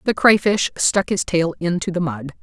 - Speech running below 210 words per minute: Yes, average, 200 wpm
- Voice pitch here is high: No, medium, 170 Hz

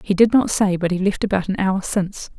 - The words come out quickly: Yes, fast, 275 wpm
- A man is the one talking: No, female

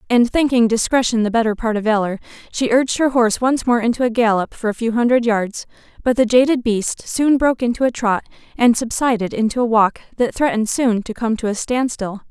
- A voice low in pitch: No, high, 235 Hz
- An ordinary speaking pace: No, fast, 215 wpm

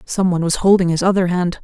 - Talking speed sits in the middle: No, fast, 220 wpm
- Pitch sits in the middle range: Yes, medium, 180 Hz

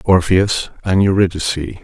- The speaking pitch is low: Yes, very low, 90 Hz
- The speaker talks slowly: Yes, slow, 100 wpm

